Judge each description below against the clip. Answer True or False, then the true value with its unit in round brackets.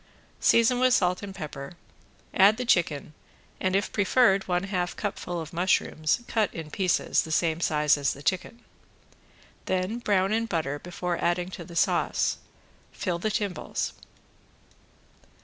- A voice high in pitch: False (180 Hz)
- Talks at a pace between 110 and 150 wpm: True (145 wpm)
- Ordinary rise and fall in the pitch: True (3.6 semitones)